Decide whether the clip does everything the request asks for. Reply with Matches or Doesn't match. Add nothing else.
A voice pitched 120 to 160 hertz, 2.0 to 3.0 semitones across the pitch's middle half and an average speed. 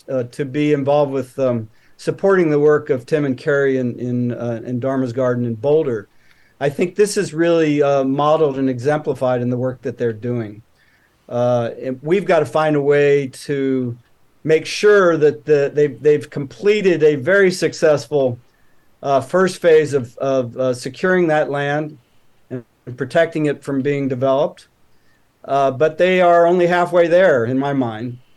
Doesn't match